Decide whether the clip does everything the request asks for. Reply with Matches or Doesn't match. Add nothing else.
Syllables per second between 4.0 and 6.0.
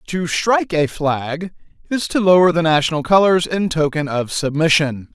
Matches